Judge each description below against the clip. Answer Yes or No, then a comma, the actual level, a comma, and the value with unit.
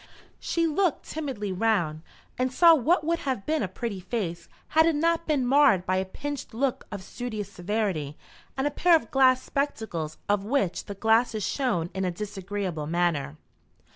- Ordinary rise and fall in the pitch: No, wide, 7.2 semitones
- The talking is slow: No, average, 170 wpm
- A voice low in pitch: No, high, 220 Hz